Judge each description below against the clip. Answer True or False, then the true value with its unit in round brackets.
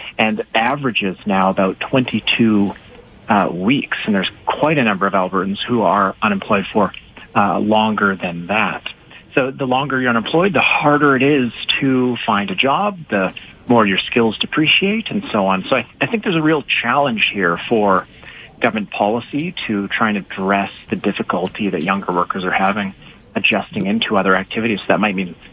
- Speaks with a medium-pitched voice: False (115 Hz)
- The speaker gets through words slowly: False (175 wpm)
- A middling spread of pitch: False (5.7 semitones)